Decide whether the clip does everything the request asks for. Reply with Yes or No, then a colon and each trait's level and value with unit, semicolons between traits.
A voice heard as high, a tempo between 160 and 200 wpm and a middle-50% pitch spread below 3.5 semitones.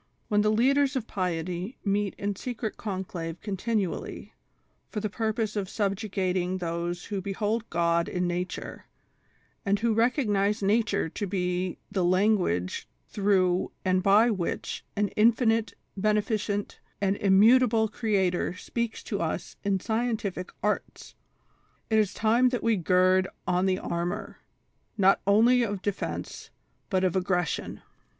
No: high, 200 Hz; slow, 135 wpm; average, 3.0 semitones